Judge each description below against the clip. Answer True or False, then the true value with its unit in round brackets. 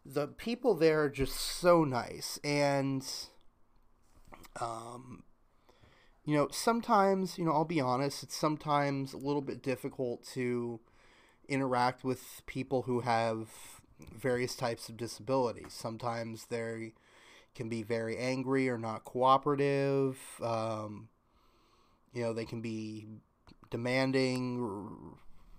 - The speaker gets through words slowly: True (115 wpm)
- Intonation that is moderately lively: True (3.4 semitones)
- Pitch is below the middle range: True (125 Hz)